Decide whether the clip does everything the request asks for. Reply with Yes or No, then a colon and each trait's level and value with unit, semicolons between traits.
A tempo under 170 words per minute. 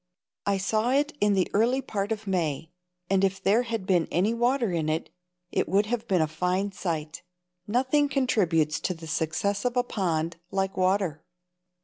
No: average, 175 wpm